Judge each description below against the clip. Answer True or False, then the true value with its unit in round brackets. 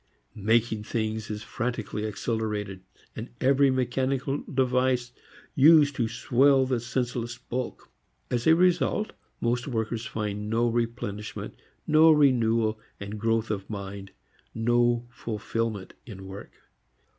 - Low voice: True (115 Hz)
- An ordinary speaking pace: False (115 wpm)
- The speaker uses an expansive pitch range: False (3.0 semitones)